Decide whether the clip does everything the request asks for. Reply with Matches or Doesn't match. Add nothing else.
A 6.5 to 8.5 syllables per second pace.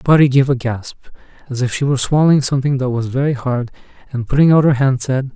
Matches